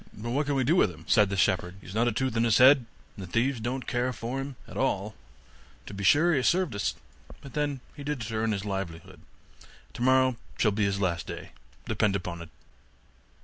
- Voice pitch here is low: Yes, low, 115 Hz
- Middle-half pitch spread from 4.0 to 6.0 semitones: Yes, average, 5.0 semitones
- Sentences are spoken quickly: Yes, fast, 230 wpm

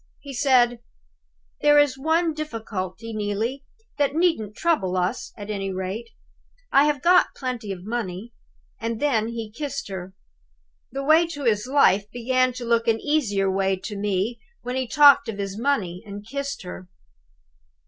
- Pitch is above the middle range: Yes, high, 230 Hz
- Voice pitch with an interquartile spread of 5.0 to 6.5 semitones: Yes, wide, 5.6 semitones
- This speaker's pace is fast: No, average, 160 wpm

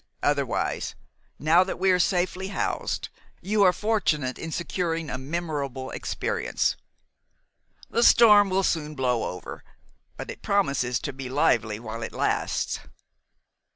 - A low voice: No, medium, 165 Hz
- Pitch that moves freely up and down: Yes, wide, 6.3 semitones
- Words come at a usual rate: No, slow, 130 wpm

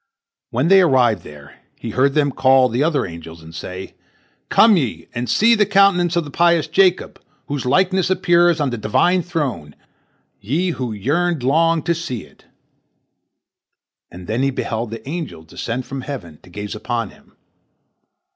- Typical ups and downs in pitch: No, wide, 7.5 semitones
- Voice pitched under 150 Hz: Yes, low, 135 Hz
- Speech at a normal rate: Yes, average, 165 wpm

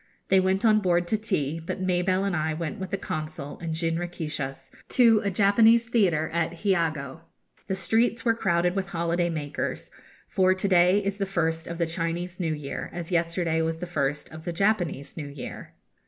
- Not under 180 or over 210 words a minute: Yes, average, 185 wpm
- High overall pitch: No, medium, 175 Hz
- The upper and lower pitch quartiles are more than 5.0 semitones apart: No, average, 3.0 semitones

